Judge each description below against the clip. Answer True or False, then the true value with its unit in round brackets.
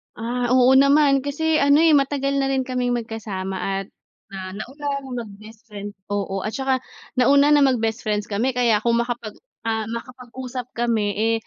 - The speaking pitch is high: True (240 Hz)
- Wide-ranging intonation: False (3.9 semitones)